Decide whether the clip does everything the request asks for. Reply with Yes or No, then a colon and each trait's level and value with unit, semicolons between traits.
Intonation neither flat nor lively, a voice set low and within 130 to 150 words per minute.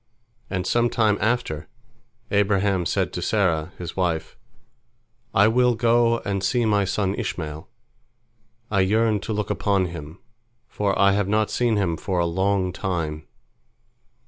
Yes: average, 3.3 semitones; low, 100 Hz; average, 145 wpm